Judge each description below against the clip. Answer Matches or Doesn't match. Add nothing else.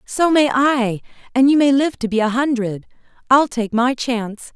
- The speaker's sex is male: Doesn't match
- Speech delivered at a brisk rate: Doesn't match